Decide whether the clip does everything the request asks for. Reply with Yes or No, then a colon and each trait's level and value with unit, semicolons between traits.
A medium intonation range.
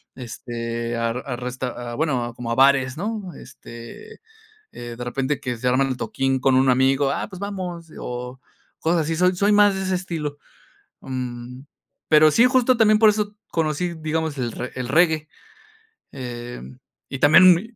No: wide, 6.2 semitones